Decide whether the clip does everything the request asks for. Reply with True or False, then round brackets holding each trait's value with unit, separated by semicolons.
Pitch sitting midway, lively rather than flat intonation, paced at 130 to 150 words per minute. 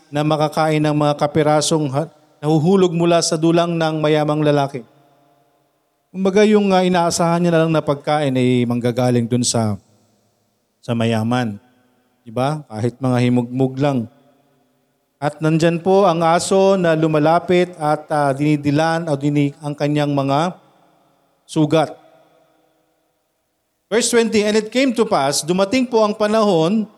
False (150 Hz; 3.5 semitones; 135 wpm)